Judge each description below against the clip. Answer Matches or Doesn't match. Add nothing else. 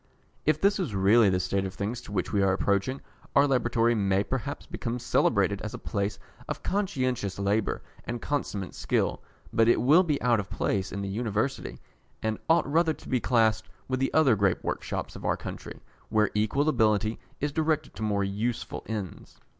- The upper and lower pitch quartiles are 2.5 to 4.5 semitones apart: Doesn't match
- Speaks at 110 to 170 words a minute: Doesn't match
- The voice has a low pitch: Matches